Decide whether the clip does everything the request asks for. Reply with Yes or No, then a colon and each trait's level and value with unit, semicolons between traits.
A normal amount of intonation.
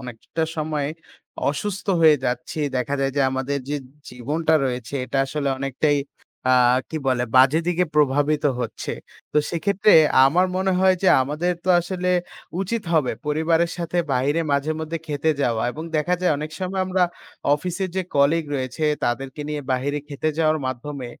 Yes: average, 3.6 semitones